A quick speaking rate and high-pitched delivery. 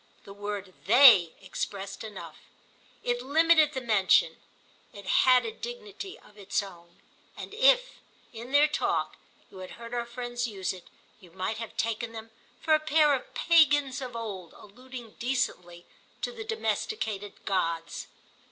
No: average, 150 wpm; high, 235 Hz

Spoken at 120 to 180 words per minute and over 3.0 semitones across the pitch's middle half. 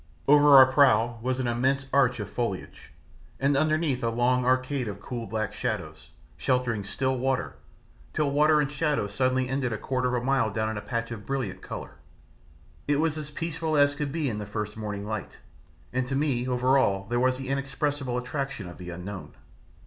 No: average, 195 wpm; average, 3.7 semitones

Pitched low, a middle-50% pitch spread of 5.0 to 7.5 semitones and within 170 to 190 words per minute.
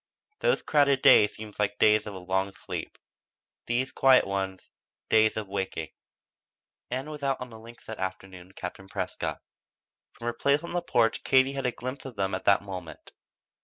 Yes: low, 110 Hz; wide, 5.4 semitones; average, 180 wpm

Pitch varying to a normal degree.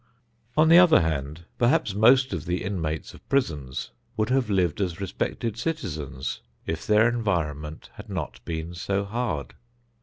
No: wide, 6.9 semitones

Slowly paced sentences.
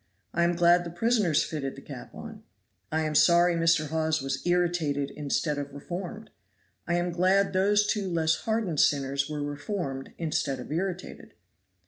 No: average, 160 wpm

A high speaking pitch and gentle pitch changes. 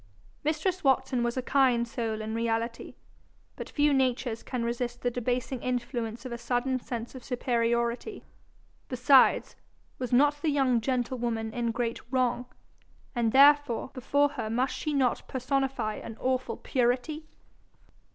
Yes: very high, 250 Hz; narrow, 2.2 semitones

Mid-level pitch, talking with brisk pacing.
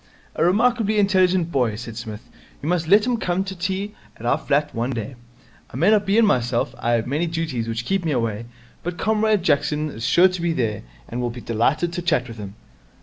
Yes: medium, 160 Hz; fast, 220 wpm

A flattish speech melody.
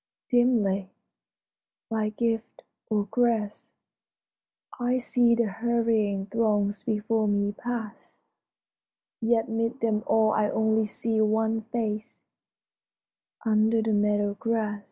Yes: narrow, 1.7 semitones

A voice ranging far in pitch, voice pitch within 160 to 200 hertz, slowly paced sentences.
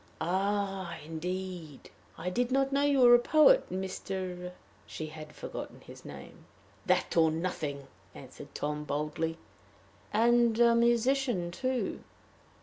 Yes: wide, 6.7 semitones; high, 190 Hz; slow, 130 wpm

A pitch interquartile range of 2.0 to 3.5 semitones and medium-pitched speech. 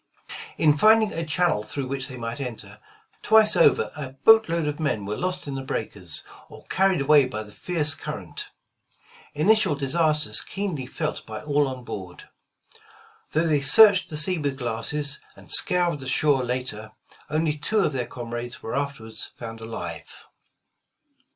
No: average, 5.1 semitones; medium, 145 Hz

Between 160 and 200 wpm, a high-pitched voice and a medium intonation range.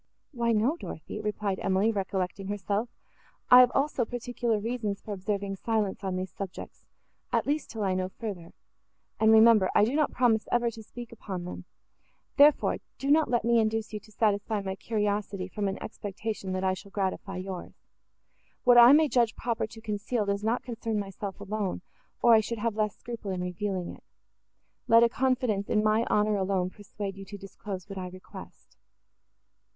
Yes: average, 180 wpm; high, 210 Hz; average, 3.0 semitones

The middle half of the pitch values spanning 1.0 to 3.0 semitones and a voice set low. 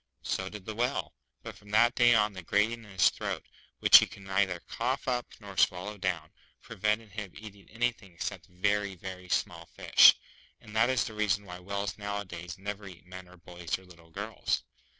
Yes: average, 2.7 semitones; low, 100 Hz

